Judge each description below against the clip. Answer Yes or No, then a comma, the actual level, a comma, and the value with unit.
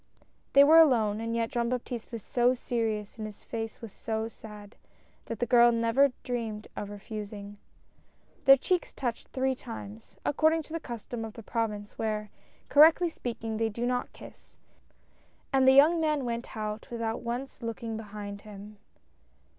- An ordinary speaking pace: Yes, average, 170 wpm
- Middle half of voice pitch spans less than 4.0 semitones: Yes, average, 2.9 semitones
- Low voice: No, high, 230 Hz